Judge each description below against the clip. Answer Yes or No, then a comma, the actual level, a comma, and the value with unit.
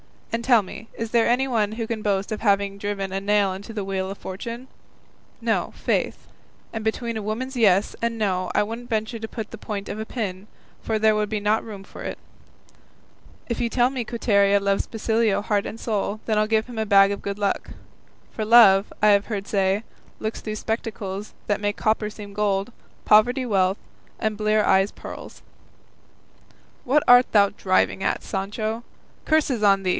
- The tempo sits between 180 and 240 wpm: Yes, average, 190 wpm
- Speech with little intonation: Yes, narrow, 2.2 semitones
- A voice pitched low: No, high, 215 Hz